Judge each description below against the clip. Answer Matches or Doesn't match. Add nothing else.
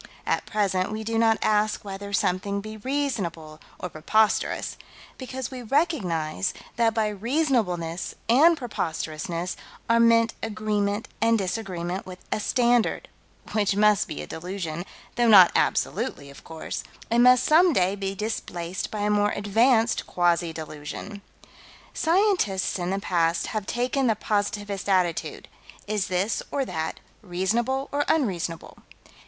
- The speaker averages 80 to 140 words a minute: Matches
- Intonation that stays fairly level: Doesn't match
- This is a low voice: Doesn't match